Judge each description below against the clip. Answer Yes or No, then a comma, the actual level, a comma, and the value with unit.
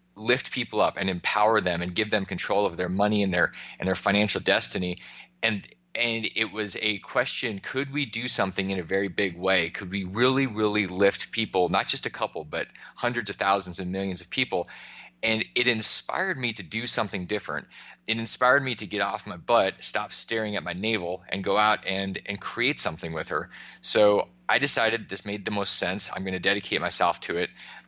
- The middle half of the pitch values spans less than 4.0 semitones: Yes, average, 2.7 semitones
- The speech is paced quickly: Yes, fast, 210 wpm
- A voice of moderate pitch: No, low, 100 Hz